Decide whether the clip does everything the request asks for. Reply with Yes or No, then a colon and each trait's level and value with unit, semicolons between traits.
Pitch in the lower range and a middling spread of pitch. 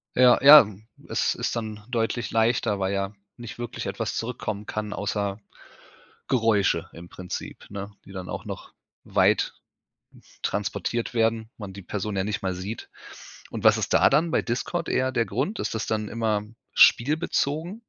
Yes: low, 110 Hz; average, 3.1 semitones